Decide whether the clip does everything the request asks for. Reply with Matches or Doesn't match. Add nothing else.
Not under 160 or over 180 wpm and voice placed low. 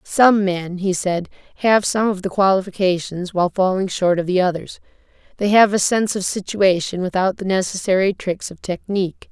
Doesn't match